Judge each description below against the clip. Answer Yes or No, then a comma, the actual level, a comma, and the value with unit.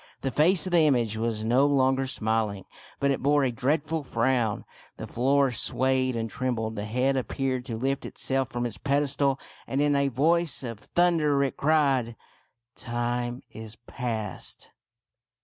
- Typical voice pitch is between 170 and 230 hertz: No, low, 130 Hz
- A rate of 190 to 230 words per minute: No, average, 165 wpm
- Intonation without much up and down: No, average, 3.1 semitones